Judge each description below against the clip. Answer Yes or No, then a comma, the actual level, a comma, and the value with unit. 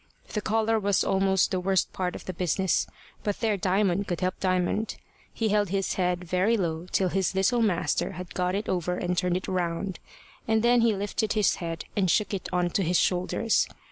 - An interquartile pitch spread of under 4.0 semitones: Yes, narrow, 2.5 semitones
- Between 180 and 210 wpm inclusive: Yes, fast, 205 wpm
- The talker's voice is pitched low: No, high, 190 Hz